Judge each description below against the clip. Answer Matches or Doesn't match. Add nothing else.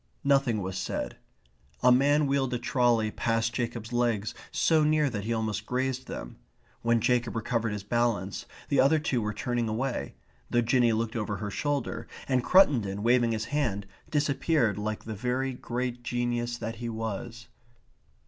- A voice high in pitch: Doesn't match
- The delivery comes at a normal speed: Matches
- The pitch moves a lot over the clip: Doesn't match